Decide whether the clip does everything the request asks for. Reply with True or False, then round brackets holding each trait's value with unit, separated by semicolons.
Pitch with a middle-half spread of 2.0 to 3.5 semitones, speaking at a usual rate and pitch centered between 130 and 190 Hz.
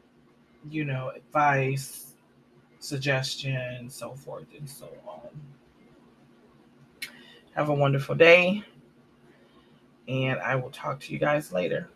False (2.8 semitones; 105 wpm; 135 Hz)